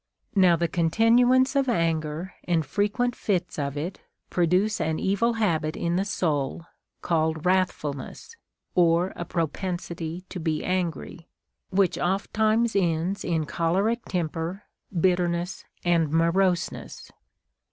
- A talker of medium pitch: Yes, medium, 175 Hz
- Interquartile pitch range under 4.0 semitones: Yes, average, 3.2 semitones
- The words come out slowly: Yes, slow, 125 wpm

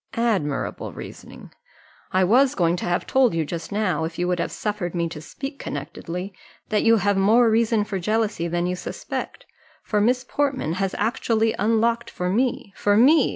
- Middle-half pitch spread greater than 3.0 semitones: Yes, average, 4.6 semitones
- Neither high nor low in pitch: No, high, 205 Hz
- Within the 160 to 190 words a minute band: Yes, average, 180 wpm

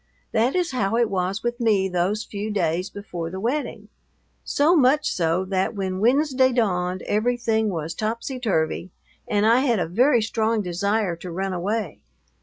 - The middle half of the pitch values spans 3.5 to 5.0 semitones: Yes, average, 4.4 semitones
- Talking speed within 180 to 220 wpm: No, average, 165 wpm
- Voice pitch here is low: No, high, 210 Hz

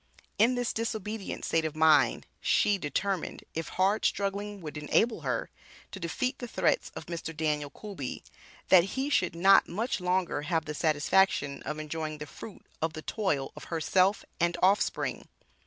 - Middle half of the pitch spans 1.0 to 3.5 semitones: No, average, 4.6 semitones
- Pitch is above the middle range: No, medium, 180 Hz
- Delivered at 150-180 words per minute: Yes, average, 160 wpm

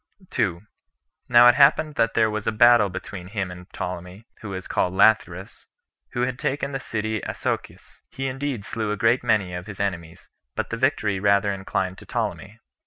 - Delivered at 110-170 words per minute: No, average, 180 wpm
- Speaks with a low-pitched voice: Yes, low, 105 Hz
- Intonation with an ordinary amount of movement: Yes, average, 4.2 semitones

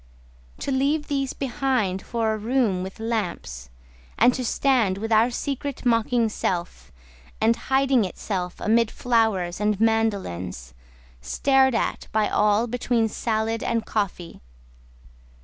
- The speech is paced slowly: Yes, slow, 125 wpm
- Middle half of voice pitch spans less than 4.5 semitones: Yes, average, 3.8 semitones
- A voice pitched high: Yes, high, 225 Hz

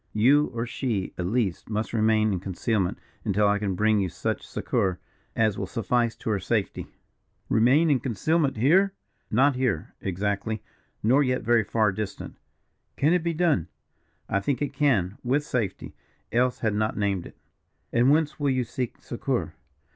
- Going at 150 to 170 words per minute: Yes, average, 165 wpm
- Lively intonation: No, average, 4.6 semitones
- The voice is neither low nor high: No, low, 115 Hz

